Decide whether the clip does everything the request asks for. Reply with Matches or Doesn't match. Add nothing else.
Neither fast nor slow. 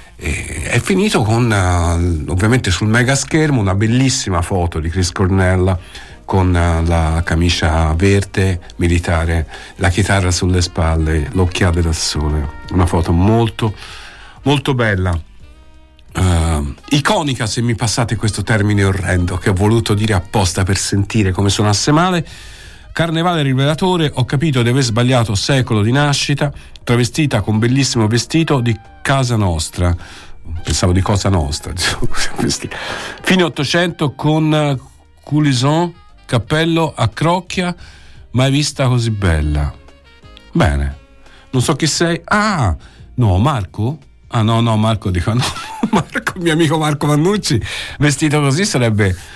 Matches